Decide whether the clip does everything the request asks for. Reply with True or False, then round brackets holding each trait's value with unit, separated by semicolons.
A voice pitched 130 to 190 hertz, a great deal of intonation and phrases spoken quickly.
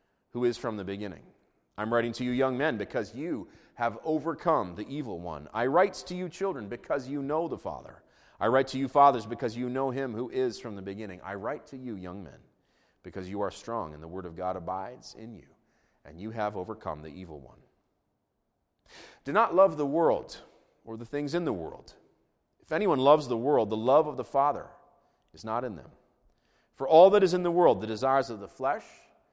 False (120 Hz; 6.4 semitones; 215 wpm)